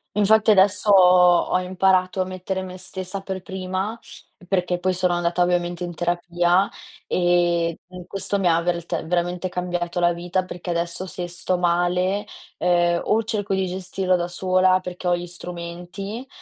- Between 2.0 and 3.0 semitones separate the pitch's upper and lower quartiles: No, narrow, 1.3 semitones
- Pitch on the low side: No, medium, 180 Hz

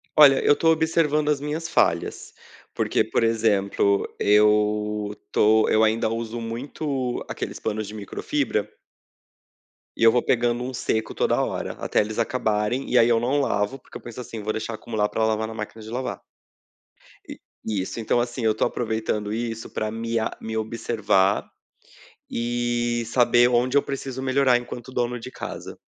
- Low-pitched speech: Yes, low, 115 Hz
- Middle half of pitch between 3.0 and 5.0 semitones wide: No, narrow, 2.5 semitones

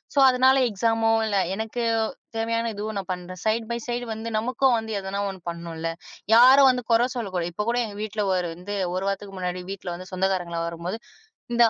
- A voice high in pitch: Yes, high, 205 Hz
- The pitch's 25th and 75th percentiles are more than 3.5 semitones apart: Yes, average, 4.0 semitones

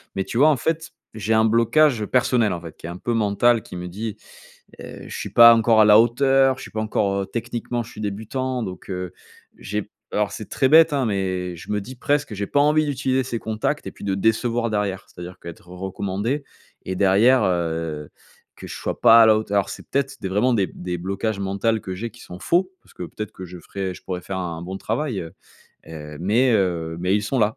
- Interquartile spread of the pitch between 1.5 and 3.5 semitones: No, average, 4.3 semitones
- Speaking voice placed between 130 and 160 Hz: No, low, 105 Hz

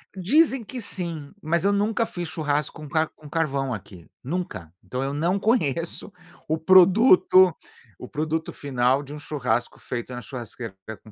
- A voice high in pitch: No, medium, 155 Hz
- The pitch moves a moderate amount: No, wide, 5.8 semitones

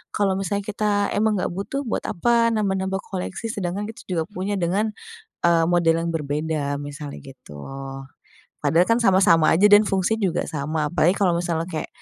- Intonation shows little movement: No, average, 4.1 semitones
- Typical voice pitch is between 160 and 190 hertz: Yes, medium, 185 Hz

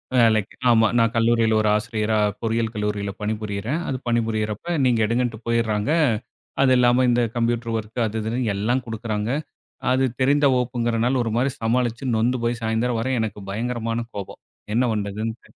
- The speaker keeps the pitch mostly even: Yes, narrow, 1.9 semitones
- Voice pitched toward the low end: Yes, low, 115 Hz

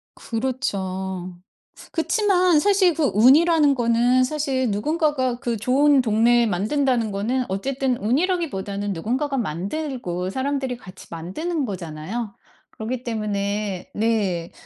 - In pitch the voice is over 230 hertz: Yes, high, 240 Hz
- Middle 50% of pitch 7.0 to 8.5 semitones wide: No, wide, 5.8 semitones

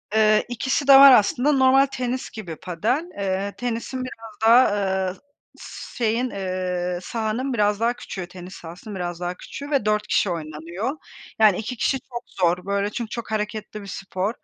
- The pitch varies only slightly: No, average, 4.6 semitones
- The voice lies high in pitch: Yes, high, 215 Hz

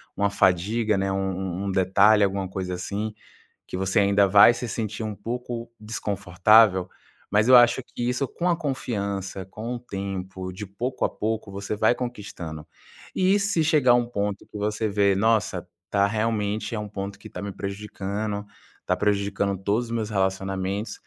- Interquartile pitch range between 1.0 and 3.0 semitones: Yes, average, 2.7 semitones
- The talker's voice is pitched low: Yes, low, 105 Hz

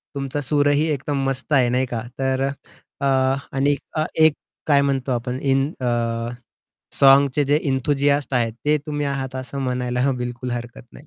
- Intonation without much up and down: Yes, narrow, 2.2 semitones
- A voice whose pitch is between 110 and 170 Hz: Yes, low, 135 Hz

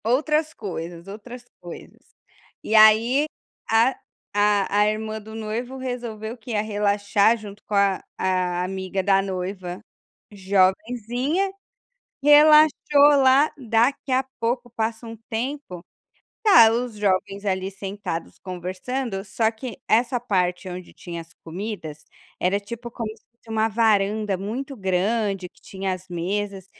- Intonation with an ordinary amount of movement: Yes, average, 3.8 semitones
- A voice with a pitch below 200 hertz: No, high, 215 Hz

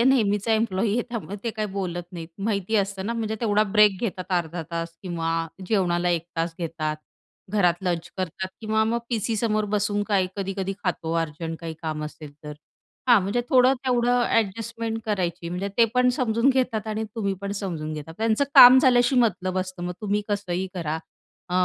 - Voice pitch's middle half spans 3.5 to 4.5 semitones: Yes, average, 4.2 semitones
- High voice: Yes, high, 200 Hz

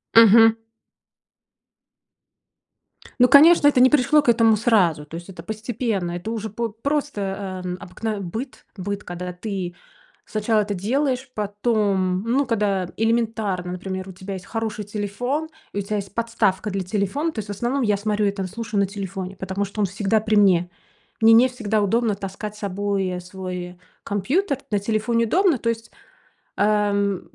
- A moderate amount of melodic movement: Yes, average, 3.1 semitones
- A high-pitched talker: Yes, high, 210 Hz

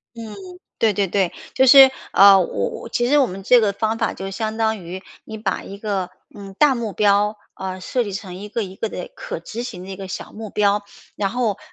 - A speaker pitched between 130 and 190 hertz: No, high, 210 Hz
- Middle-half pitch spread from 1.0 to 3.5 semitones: Yes, average, 2.7 semitones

